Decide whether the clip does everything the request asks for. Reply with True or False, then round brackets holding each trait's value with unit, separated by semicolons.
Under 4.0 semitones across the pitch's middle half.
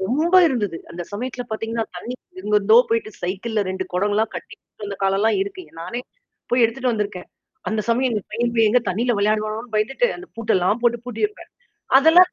True (3.3 semitones)